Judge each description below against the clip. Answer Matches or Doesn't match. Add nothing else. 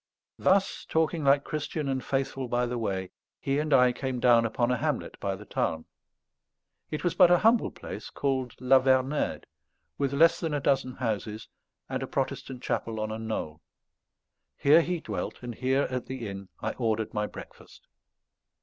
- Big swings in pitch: Doesn't match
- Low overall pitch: Matches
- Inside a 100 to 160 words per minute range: Doesn't match